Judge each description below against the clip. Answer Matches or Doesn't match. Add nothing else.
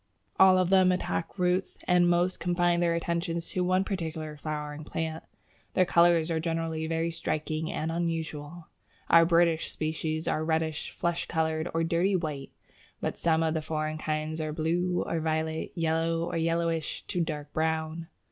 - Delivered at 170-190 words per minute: Doesn't match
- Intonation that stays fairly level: Matches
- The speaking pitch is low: Doesn't match